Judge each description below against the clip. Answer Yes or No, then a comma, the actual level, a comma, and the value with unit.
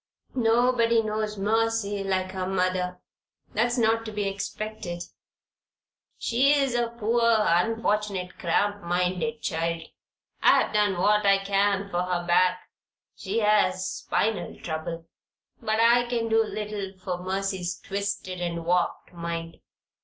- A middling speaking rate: No, slow, 125 wpm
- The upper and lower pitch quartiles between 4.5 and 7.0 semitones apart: No, average, 3.6 semitones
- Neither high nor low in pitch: No, high, 200 Hz